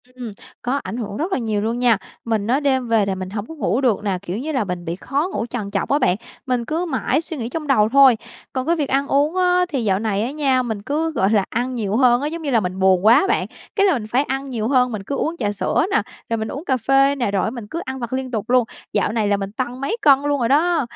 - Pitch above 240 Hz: Yes, very high, 250 Hz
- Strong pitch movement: No, average, 4.7 semitones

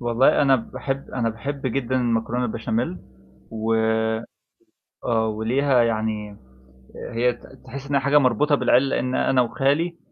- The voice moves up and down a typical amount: Yes, average, 3.3 semitones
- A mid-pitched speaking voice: No, low, 125 Hz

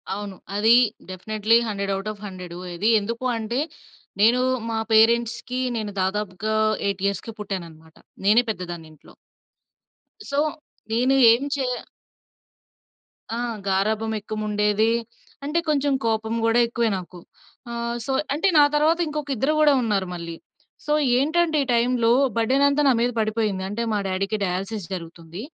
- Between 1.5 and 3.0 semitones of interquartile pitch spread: No, average, 3.6 semitones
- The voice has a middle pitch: No, high, 220 Hz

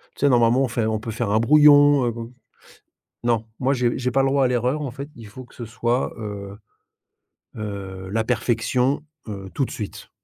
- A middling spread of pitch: Yes, average, 3.2 semitones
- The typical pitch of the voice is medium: No, low, 120 Hz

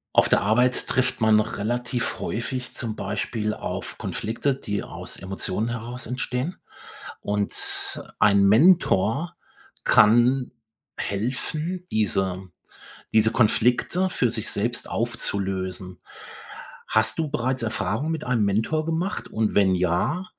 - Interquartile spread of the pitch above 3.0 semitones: Yes, average, 3.8 semitones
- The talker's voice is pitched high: No, low, 115 Hz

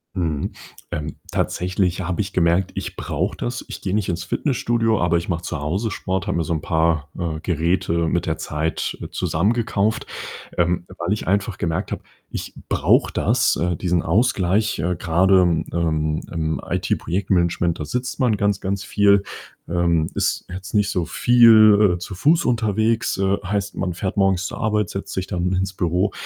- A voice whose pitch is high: No, very low, 90 Hz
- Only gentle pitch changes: No, average, 3.3 semitones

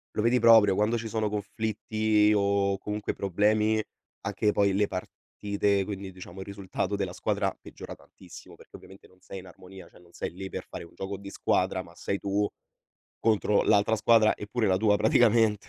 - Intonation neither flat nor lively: No, narrow, 1.9 semitones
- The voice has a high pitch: No, low, 100 Hz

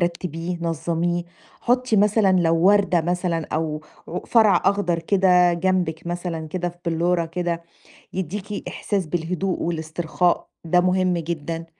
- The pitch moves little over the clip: Yes, narrow, 2.0 semitones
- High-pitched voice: No, medium, 175 Hz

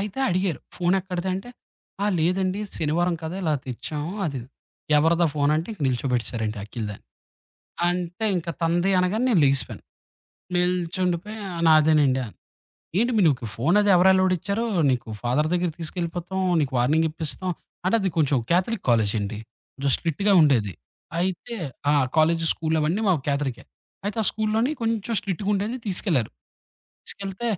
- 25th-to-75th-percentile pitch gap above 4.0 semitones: Yes, average, 4.5 semitones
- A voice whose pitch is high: No, medium, 175 Hz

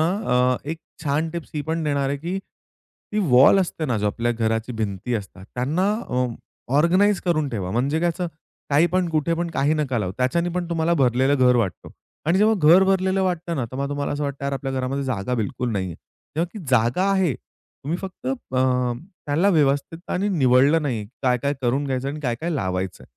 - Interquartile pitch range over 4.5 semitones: Yes, average, 5.1 semitones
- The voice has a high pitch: No, medium, 140 Hz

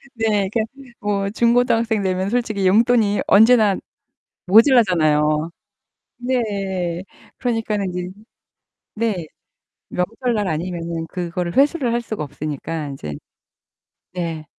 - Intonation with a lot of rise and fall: No, average, 5.0 semitones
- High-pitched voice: Yes, high, 200 Hz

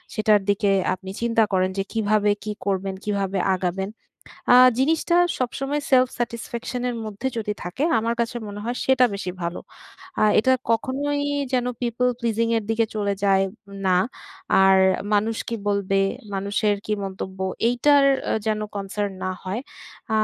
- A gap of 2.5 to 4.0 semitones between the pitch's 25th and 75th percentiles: Yes, average, 3.5 semitones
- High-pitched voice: Yes, high, 215 Hz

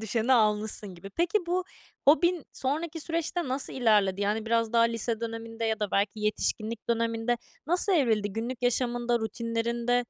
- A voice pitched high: Yes, high, 230 Hz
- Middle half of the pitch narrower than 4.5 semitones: Yes, average, 2.9 semitones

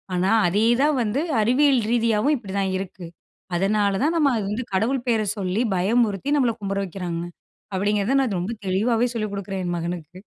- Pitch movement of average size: Yes, average, 4.1 semitones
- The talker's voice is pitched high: Yes, high, 210 Hz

